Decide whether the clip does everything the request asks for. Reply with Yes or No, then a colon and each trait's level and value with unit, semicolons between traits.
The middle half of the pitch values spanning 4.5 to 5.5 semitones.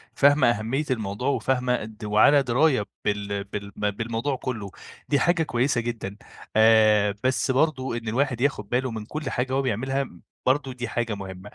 No: average, 3.9 semitones